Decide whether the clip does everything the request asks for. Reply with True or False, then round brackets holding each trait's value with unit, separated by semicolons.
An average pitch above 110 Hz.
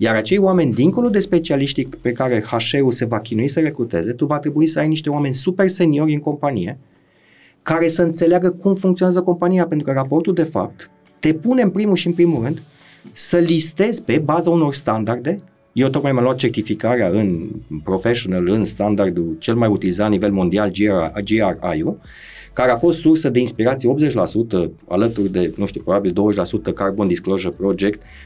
True (140 Hz)